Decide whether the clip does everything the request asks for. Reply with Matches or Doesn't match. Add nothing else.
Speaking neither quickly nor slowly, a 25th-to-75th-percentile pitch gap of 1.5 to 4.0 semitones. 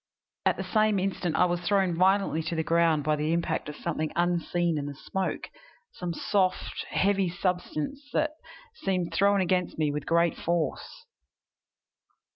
Matches